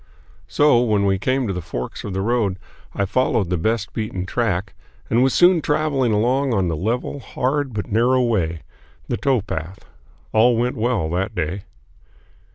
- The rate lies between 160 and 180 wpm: Yes, average, 165 wpm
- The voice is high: No, low, 110 Hz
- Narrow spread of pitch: No, average, 4.8 semitones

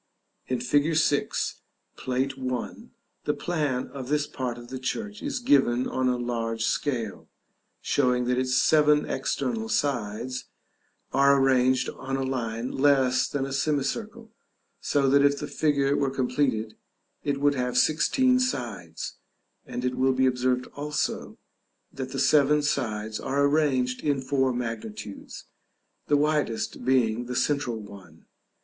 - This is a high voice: No, low, 130 Hz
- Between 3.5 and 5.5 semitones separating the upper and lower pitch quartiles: No, narrow, 2.5 semitones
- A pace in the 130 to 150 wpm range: Yes, average, 140 wpm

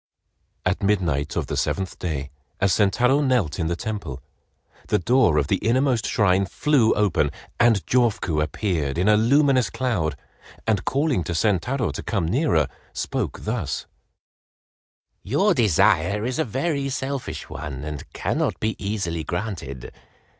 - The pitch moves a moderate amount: No, wide, 7.1 semitones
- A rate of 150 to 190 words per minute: No, average, 140 wpm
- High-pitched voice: No, low, 105 Hz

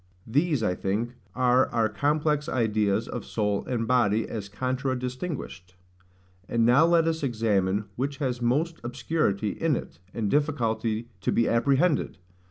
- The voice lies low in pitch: Yes, low, 120 Hz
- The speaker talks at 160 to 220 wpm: No, average, 140 wpm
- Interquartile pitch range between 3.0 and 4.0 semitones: No, average, 4.7 semitones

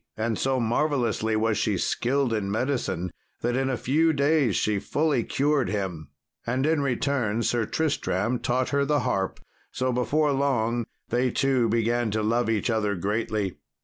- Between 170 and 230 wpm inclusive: No, average, 160 wpm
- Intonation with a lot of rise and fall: No, average, 4.0 semitones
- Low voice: Yes, low, 120 Hz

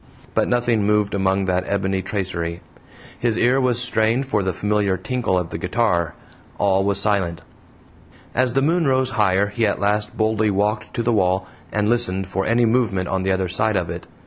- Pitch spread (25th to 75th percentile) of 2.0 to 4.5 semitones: Yes, average, 3.6 semitones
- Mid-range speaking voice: No, low, 105 Hz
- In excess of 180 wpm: Yes, average, 190 wpm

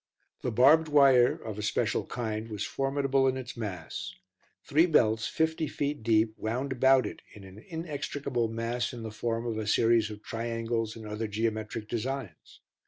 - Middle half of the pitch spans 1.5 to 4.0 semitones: Yes, average, 3.6 semitones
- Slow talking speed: No, average, 170 wpm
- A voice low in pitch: Yes, low, 115 Hz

